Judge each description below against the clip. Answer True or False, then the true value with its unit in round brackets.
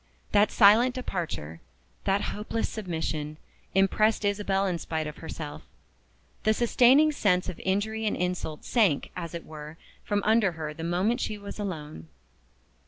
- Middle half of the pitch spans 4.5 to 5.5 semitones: True (4.9 semitones)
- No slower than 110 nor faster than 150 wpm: True (145 wpm)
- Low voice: False (195 Hz)